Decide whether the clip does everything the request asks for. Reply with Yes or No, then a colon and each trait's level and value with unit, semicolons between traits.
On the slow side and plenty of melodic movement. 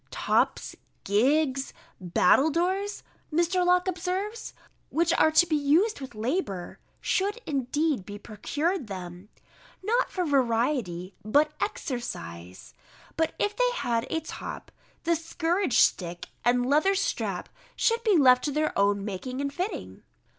Yes: slow, 130 wpm; wide, 7.9 semitones